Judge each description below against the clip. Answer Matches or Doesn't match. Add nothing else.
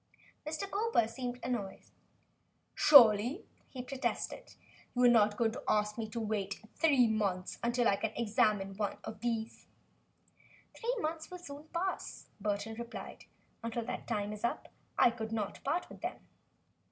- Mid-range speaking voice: Doesn't match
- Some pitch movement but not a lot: Matches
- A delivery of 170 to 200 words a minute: Doesn't match